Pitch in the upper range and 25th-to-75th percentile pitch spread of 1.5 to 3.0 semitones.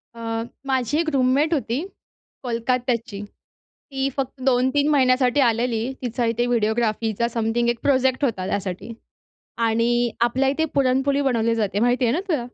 Yes: high, 245 Hz; narrow, 2.6 semitones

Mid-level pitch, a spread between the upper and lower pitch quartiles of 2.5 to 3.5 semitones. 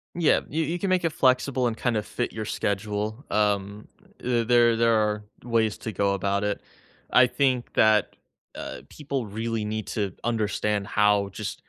No: low, 110 Hz; average, 2.9 semitones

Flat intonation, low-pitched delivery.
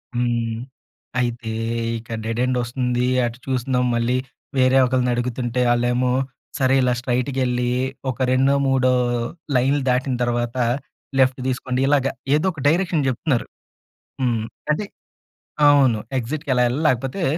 Yes: narrow, 1.7 semitones; low, 125 Hz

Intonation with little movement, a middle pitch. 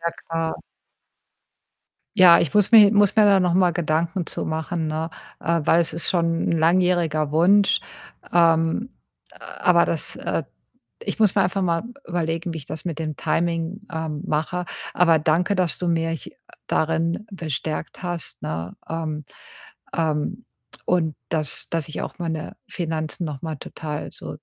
Yes: narrow, 2.1 semitones; medium, 165 Hz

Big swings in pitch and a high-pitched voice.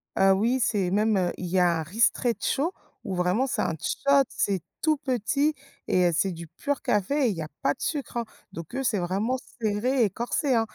Yes: wide, 6.1 semitones; high, 215 Hz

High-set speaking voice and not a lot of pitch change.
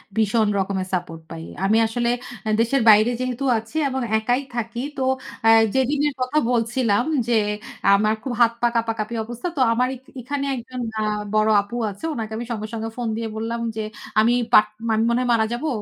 Yes: high, 230 Hz; narrow, 2.3 semitones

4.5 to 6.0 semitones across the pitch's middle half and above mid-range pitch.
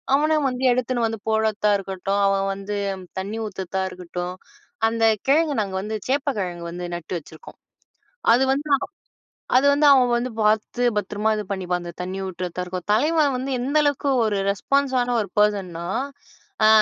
Yes: average, 5.3 semitones; high, 210 Hz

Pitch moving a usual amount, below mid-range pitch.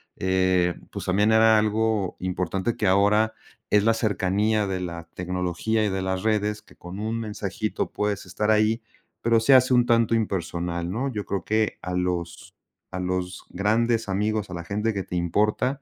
Yes: average, 3.3 semitones; low, 105 Hz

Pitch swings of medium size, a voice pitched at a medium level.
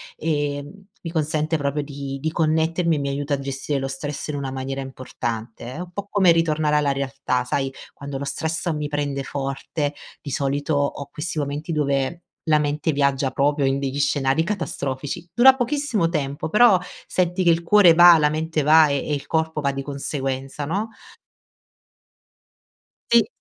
Yes: average, 3.0 semitones; medium, 145 Hz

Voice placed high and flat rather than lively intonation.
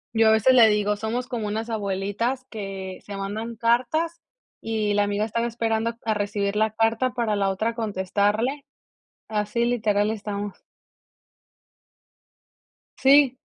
Yes: high, 220 Hz; narrow, 2.3 semitones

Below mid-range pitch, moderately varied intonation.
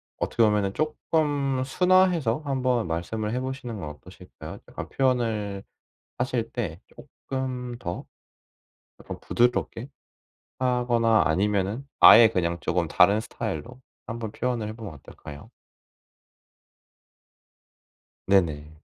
Yes: low, 115 Hz; average, 4.6 semitones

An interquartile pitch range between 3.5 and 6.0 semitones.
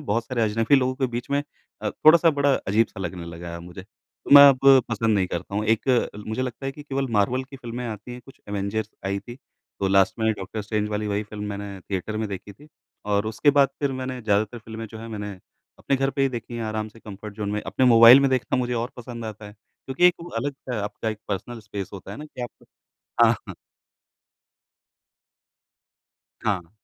Yes: average, 3.8 semitones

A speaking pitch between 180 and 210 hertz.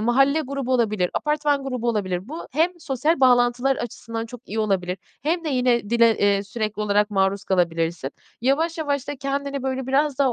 No: high, 245 Hz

